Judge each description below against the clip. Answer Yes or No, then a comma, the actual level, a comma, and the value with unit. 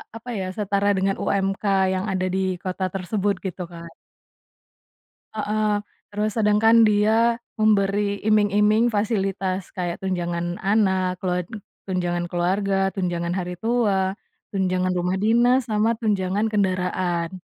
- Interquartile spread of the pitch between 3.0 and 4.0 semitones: No, narrow, 2.5 semitones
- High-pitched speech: Yes, high, 195 Hz